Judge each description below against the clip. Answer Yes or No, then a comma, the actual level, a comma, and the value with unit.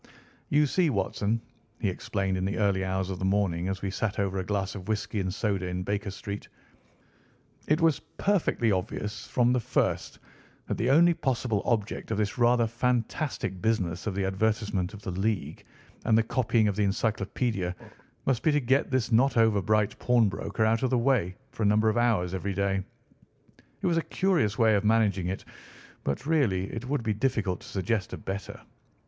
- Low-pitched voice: Yes, low, 105 Hz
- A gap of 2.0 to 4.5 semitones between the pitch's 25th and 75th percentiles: Yes, average, 3.6 semitones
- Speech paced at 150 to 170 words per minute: No, average, 190 wpm